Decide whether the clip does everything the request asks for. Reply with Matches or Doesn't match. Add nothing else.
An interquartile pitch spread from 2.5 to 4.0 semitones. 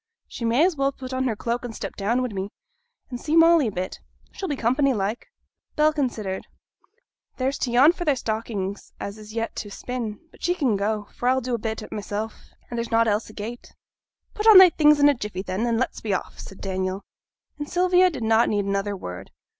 Doesn't match